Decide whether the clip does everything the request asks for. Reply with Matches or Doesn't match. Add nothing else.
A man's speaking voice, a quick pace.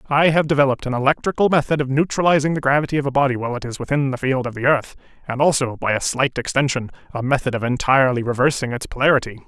Matches